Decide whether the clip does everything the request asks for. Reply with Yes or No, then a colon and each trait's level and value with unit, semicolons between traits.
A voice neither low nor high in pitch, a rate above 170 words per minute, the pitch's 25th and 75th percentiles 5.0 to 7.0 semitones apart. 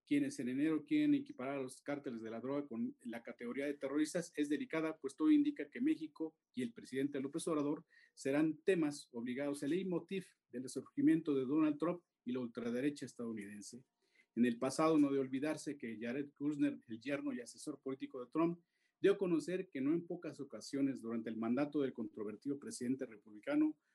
No: medium, 145 Hz; average, 185 wpm; average, 4.5 semitones